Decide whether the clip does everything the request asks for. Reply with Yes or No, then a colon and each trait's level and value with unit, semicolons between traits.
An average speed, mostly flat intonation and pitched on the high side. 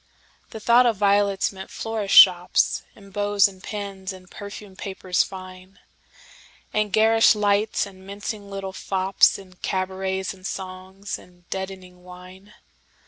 No: slow, 120 wpm; narrow, 1.5 semitones; high, 195 Hz